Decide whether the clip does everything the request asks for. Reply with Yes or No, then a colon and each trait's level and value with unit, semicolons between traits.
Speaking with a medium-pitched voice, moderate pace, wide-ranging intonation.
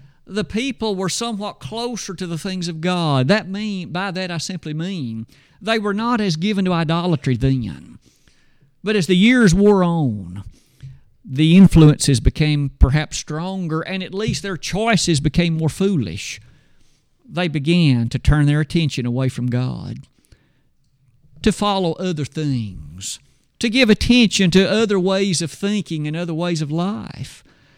Yes: medium, 170 Hz; average, 150 wpm; wide, 5.7 semitones